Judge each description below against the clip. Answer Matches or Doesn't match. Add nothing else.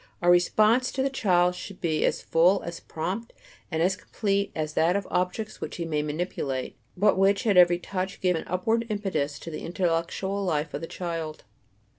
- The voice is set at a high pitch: Doesn't match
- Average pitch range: Matches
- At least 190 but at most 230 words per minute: Matches